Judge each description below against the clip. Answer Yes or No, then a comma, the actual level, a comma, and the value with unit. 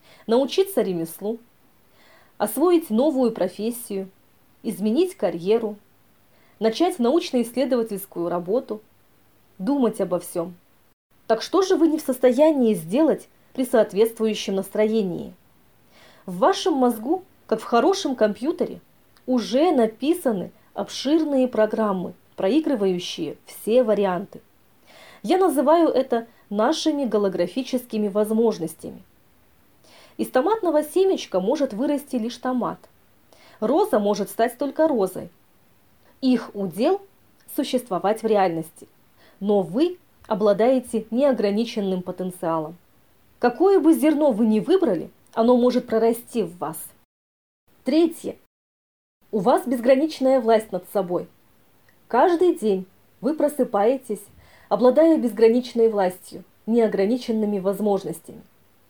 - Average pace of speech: No, slow, 95 wpm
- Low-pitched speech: No, high, 230 Hz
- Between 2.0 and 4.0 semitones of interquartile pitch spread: No, average, 5.3 semitones